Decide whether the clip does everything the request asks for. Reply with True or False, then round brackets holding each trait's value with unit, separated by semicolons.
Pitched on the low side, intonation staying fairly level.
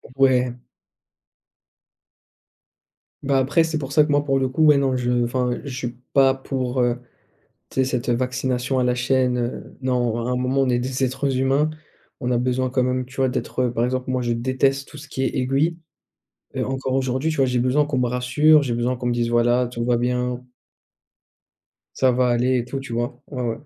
True (130 Hz; 1.4 semitones)